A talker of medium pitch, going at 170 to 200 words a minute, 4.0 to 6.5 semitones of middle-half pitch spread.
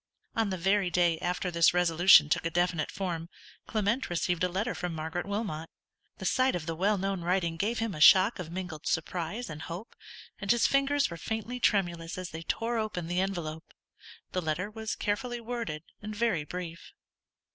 Yes: medium, 180 Hz; average, 185 wpm; average, 4.3 semitones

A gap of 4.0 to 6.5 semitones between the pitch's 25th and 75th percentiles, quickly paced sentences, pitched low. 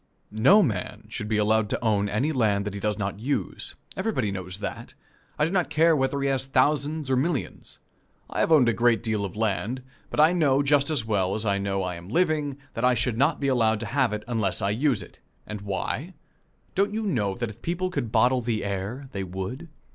Yes: wide, 5.4 semitones; fast, 225 wpm; low, 120 Hz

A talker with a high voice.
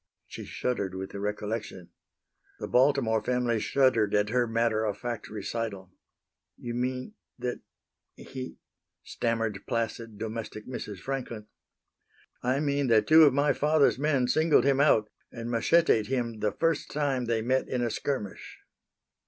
No: low, 120 Hz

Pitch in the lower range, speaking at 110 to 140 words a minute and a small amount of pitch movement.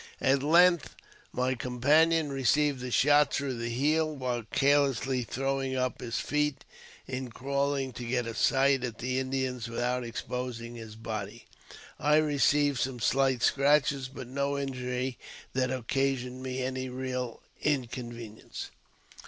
Yes: low, 130 Hz; slow, 135 wpm; narrow, 2.1 semitones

